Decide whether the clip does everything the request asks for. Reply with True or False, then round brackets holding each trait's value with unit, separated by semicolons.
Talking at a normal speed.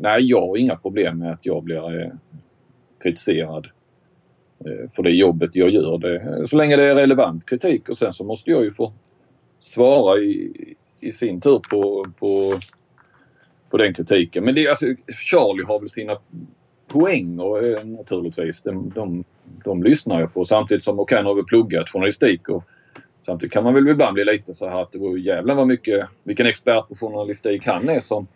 True (180 wpm)